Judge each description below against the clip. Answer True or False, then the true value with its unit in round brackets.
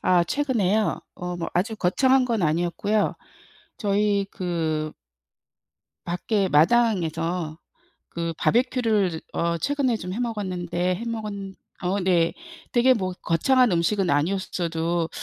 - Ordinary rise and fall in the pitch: True (4.6 semitones)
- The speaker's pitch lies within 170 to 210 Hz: True (185 Hz)